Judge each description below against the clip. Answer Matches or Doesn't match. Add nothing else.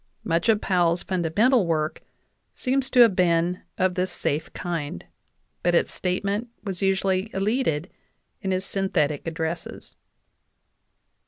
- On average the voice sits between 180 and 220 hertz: Matches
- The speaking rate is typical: Doesn't match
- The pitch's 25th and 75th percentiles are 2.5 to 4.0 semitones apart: Matches